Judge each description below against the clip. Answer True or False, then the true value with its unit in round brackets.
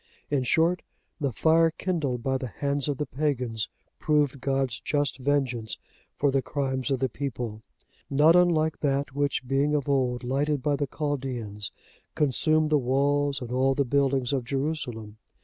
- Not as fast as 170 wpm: True (160 wpm)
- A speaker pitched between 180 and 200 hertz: False (140 Hz)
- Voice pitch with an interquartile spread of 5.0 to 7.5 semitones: False (2.5 semitones)